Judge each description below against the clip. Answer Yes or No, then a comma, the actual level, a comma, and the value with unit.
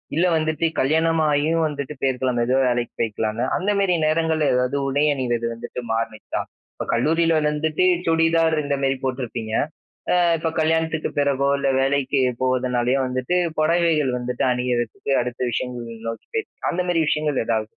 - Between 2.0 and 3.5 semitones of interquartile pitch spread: No, average, 4.4 semitones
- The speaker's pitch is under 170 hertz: Yes, medium, 140 Hz